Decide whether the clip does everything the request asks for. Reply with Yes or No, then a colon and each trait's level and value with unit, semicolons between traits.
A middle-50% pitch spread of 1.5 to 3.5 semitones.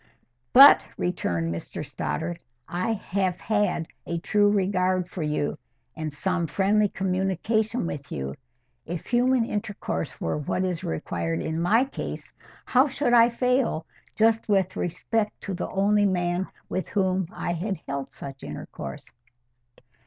No: average, 4.4 semitones